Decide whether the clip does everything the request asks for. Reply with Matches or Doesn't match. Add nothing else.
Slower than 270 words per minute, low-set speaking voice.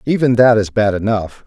Matches